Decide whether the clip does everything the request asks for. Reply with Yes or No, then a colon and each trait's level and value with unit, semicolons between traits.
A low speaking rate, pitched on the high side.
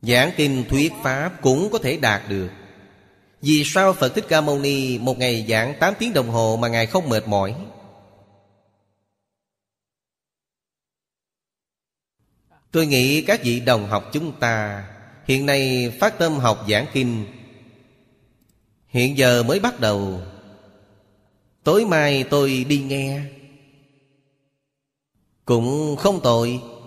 No: slow, 125 wpm; low, 125 Hz